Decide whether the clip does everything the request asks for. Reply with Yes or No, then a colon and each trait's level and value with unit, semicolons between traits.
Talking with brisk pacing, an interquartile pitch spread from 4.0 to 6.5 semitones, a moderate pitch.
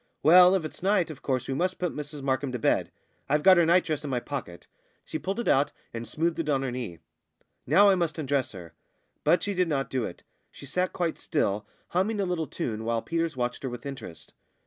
Yes: fast, 225 wpm; wide, 5.5 semitones; medium, 150 Hz